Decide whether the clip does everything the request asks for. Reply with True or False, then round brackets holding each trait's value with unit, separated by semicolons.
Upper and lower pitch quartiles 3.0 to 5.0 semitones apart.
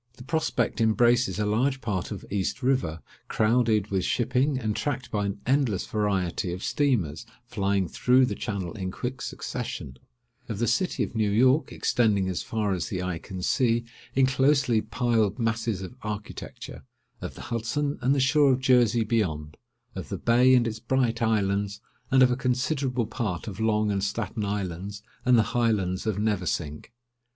True (4.0 semitones)